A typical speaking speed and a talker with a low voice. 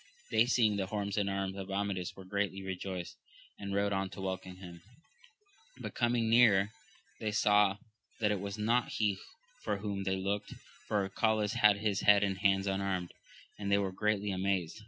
Yes: average, 180 wpm; low, 100 Hz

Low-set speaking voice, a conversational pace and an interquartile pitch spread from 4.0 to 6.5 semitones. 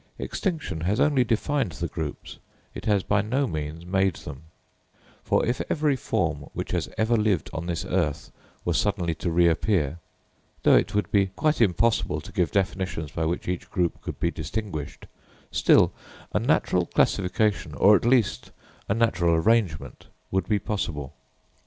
Yes: very low, 95 Hz; average, 160 wpm; average, 4.9 semitones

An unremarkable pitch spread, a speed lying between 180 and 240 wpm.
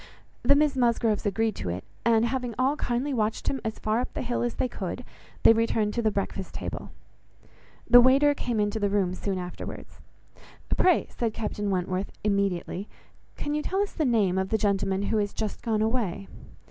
Yes: average, 3.6 semitones; average, 190 wpm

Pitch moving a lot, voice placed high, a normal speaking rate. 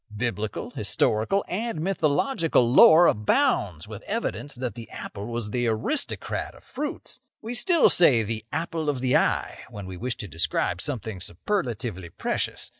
No: wide, 8.5 semitones; low, 125 Hz; average, 150 wpm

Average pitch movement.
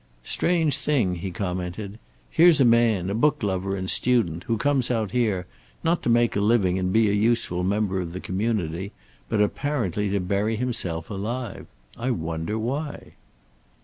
Yes: average, 4.3 semitones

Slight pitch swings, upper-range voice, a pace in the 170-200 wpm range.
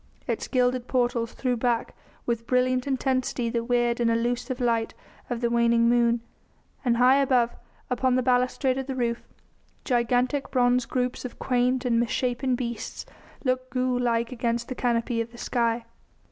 No: narrow, 1.4 semitones; high, 245 Hz; average, 160 wpm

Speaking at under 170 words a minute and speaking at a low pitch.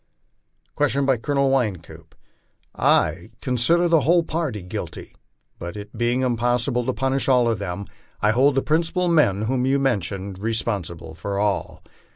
Yes: average, 155 wpm; low, 120 Hz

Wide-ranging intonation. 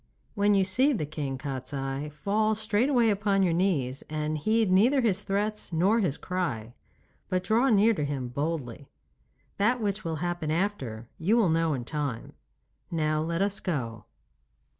Yes: wide, 6.1 semitones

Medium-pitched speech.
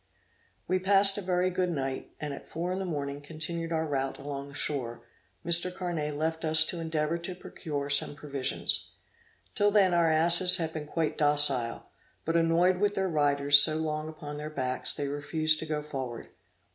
Yes: medium, 155 Hz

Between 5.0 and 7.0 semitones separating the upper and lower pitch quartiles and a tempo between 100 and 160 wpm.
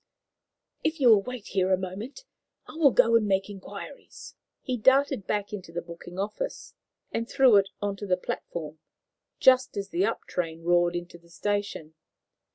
No: average, 5.3 semitones; average, 170 wpm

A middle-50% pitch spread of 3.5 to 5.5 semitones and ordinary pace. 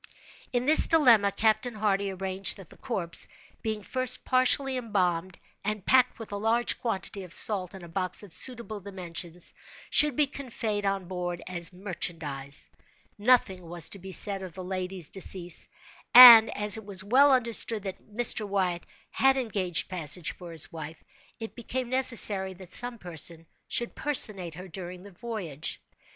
Yes: average, 4.5 semitones; average, 160 wpm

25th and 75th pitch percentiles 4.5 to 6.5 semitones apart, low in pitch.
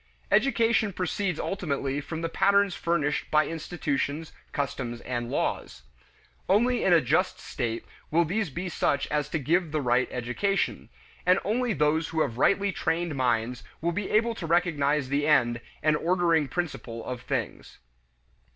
No: average, 4.8 semitones; medium, 160 Hz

